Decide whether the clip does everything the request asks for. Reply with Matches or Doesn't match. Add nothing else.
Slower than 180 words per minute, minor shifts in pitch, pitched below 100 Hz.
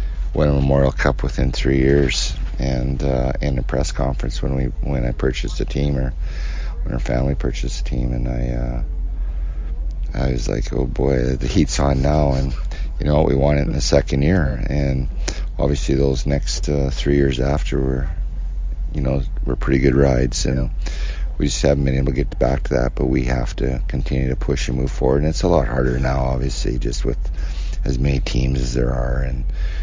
Doesn't match